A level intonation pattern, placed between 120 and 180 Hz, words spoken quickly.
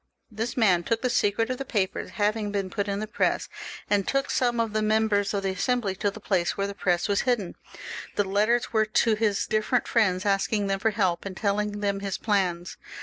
No: narrow, 2.1 semitones; high, 205 Hz; fast, 220 wpm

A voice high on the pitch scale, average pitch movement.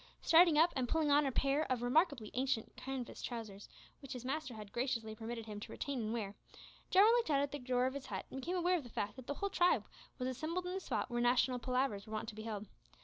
Yes: very high, 255 Hz; average, 4.5 semitones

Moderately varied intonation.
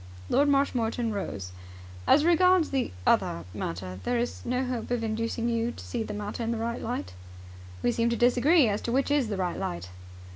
Yes: average, 3.5 semitones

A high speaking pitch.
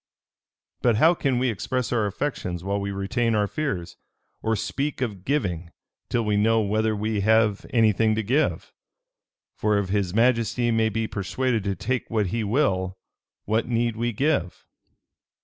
No: low, 110 Hz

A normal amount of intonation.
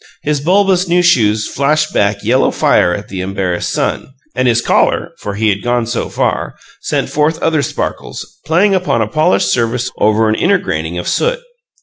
No: wide, 7.4 semitones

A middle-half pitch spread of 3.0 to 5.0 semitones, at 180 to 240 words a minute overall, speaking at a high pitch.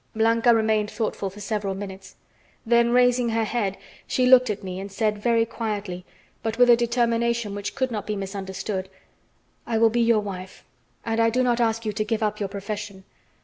No: narrow, 2.6 semitones; average, 190 wpm; high, 220 Hz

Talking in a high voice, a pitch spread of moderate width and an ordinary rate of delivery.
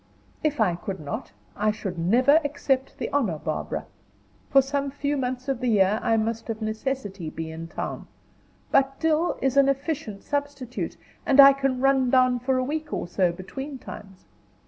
Yes: very high, 255 Hz; average, 4.8 semitones; average, 175 wpm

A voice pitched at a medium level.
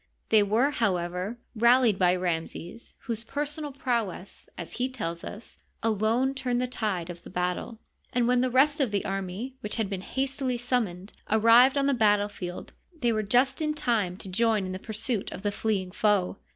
No: high, 220 Hz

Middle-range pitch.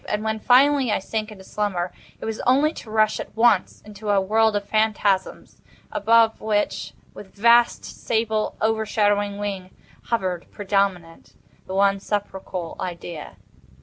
No: high, 210 Hz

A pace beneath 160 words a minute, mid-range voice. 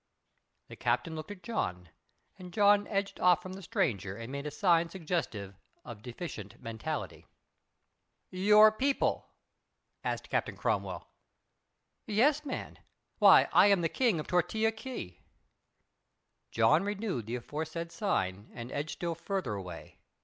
Yes: slow, 135 wpm; medium, 170 Hz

